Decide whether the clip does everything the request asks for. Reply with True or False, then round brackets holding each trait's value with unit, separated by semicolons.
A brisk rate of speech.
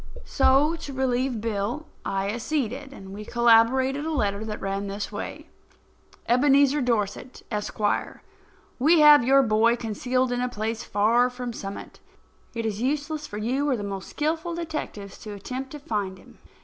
False (160 wpm)